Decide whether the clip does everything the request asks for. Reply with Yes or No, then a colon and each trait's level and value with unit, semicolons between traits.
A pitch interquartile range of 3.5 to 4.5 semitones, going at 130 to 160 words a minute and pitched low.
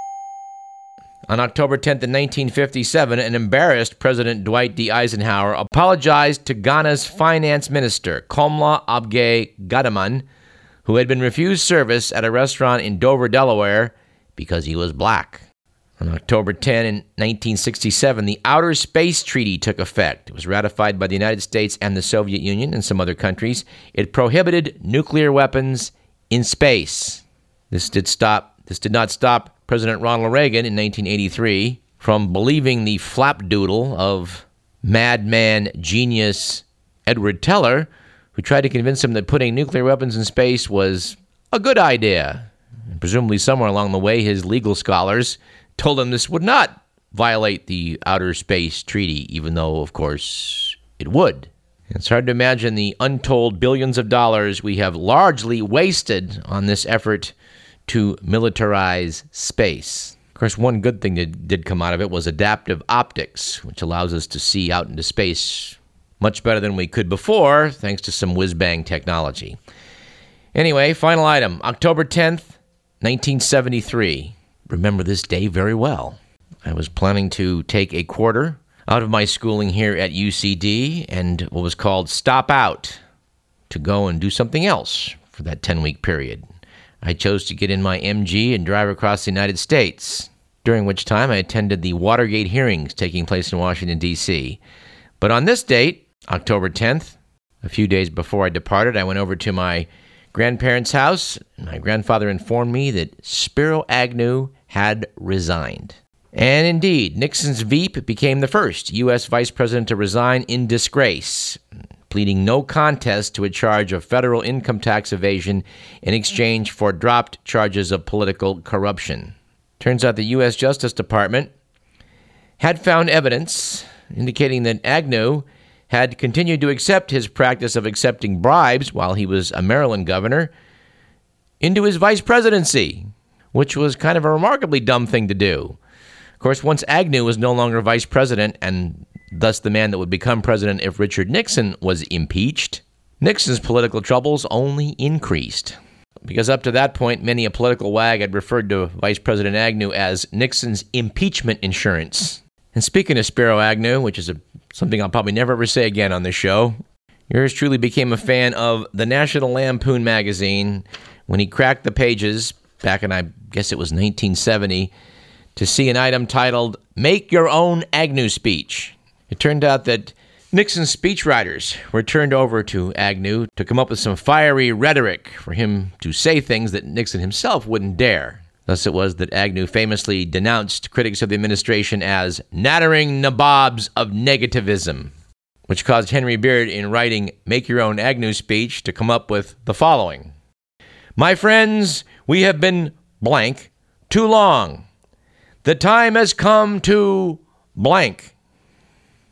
No: average, 5.0 semitones; average, 155 wpm; low, 110 Hz